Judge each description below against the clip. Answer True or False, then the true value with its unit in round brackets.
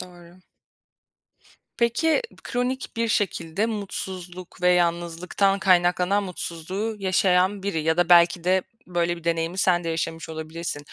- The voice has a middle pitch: True (180 Hz)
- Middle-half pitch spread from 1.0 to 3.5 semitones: True (2.5 semitones)